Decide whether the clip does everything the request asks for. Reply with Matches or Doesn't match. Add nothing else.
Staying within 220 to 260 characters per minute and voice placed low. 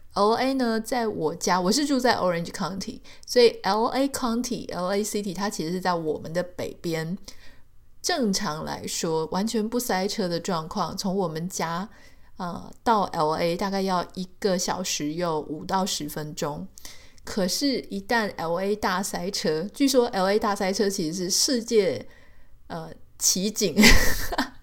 Doesn't match